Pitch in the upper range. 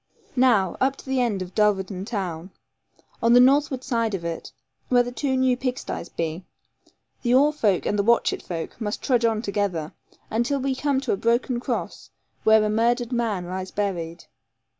Yes: high, 225 Hz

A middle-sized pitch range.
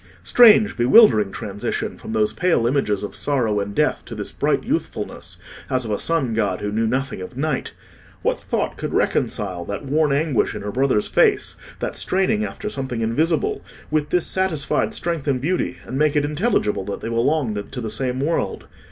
No: wide, 6.4 semitones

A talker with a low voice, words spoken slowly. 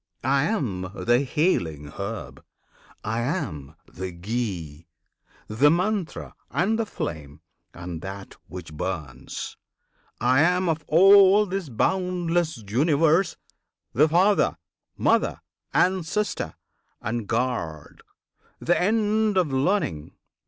Yes: low, 130 Hz; slow, 105 wpm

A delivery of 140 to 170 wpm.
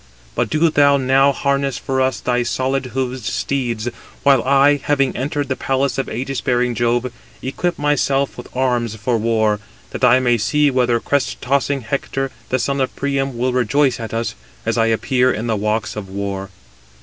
No: average, 185 wpm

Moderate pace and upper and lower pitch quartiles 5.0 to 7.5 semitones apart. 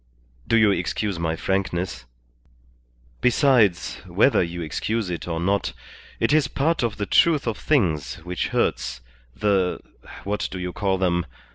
No: average, 145 wpm; average, 4.2 semitones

